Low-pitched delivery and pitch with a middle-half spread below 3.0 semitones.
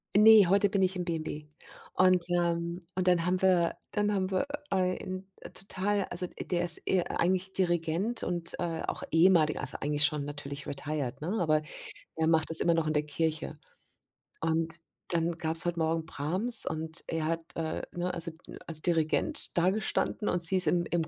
No: medium, 170 Hz; narrow, 2.5 semitones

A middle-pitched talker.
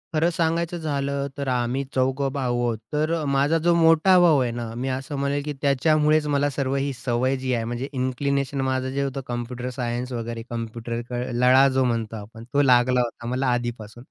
No: low, 130 Hz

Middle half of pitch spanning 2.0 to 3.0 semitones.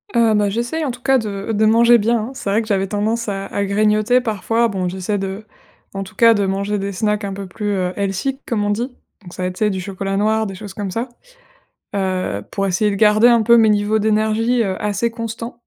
Yes: average, 2.7 semitones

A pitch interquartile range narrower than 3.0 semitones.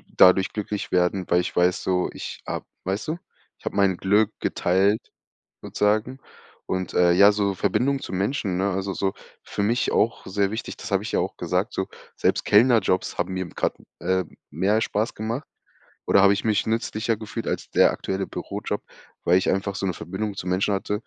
Yes: narrow, 2.5 semitones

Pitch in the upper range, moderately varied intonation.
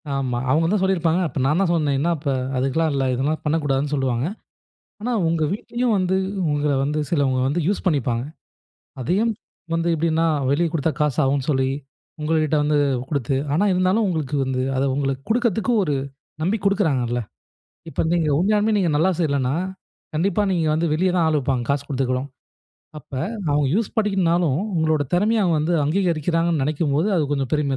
No: medium, 155 Hz; average, 4.2 semitones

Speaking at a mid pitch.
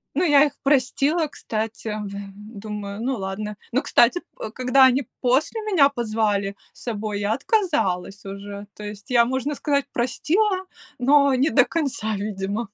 No: high, 240 Hz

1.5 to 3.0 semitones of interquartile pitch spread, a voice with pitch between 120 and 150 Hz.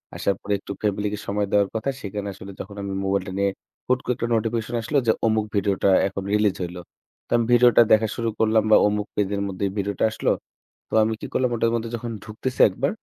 No: narrow, 2.4 semitones; low, 105 Hz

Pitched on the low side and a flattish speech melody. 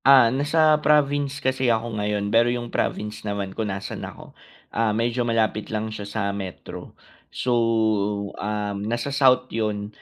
No: low, 115 Hz; average, 3.9 semitones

